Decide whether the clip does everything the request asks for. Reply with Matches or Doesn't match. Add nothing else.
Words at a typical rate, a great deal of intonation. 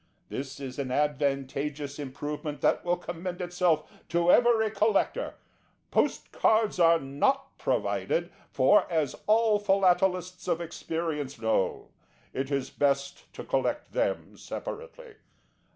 Doesn't match